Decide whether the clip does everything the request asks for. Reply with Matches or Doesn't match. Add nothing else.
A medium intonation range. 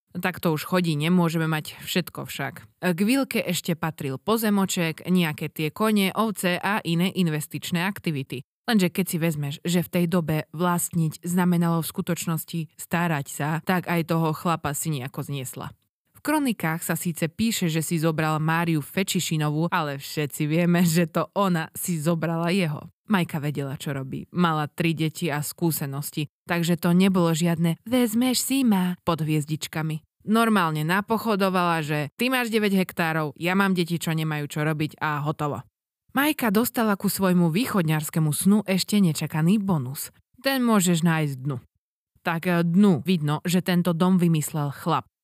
Matches